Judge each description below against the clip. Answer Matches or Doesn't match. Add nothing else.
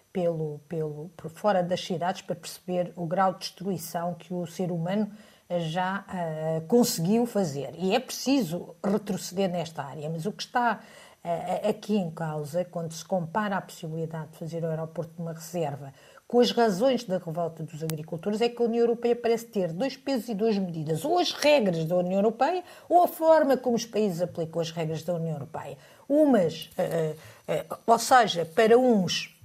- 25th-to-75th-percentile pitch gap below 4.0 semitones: Doesn't match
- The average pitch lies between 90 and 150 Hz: Doesn't match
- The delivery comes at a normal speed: Doesn't match